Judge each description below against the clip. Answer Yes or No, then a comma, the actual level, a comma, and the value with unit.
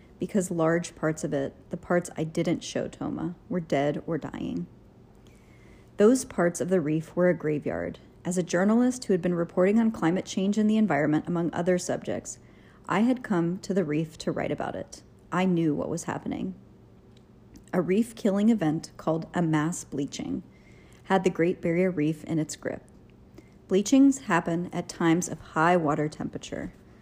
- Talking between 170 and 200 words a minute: Yes, average, 175 wpm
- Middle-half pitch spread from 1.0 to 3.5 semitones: Yes, average, 3.2 semitones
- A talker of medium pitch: Yes, medium, 175 Hz